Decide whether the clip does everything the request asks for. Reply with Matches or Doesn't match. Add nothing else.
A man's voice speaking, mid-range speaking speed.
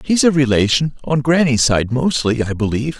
Matches